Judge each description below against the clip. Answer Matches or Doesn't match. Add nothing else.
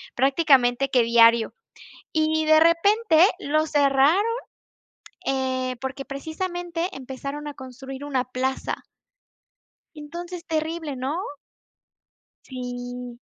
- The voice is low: Doesn't match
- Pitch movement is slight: Doesn't match